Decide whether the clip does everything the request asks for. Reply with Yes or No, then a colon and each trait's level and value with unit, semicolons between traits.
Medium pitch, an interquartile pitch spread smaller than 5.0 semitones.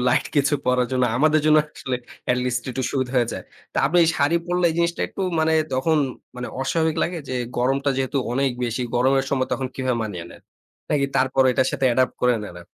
No: low, 130 Hz; average, 2.9 semitones